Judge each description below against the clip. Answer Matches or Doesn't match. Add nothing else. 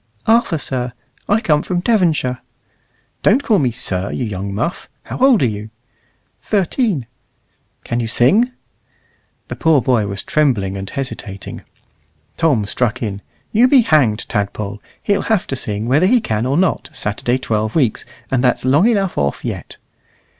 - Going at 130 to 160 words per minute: Matches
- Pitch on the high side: Doesn't match